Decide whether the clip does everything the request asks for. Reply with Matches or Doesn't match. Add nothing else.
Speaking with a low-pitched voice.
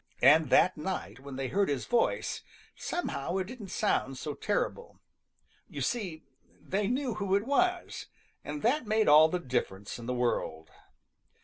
Doesn't match